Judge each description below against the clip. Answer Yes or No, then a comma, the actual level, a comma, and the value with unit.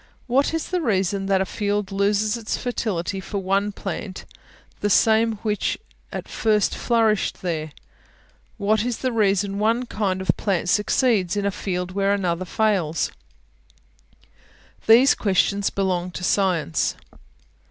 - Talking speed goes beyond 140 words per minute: No, slow, 135 wpm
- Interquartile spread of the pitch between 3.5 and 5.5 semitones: No, narrow, 2.6 semitones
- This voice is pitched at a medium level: No, high, 200 Hz